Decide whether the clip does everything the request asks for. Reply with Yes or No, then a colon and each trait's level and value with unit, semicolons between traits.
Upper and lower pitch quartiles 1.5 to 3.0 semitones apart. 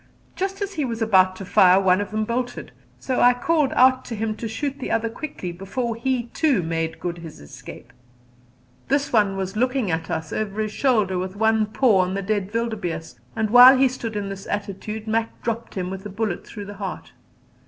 No: average, 4.3 semitones